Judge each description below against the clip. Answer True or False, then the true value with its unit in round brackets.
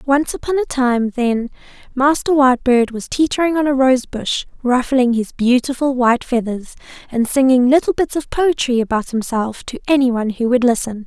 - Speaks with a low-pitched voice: False (255 Hz)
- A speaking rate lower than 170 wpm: False (175 wpm)